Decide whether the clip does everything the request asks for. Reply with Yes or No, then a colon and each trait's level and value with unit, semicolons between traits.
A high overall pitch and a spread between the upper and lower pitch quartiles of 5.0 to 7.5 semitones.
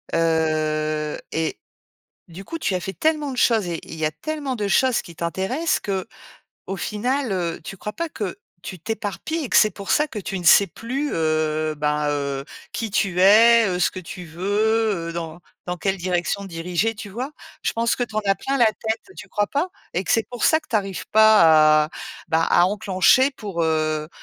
Yes: high, 195 Hz; wide, 5.4 semitones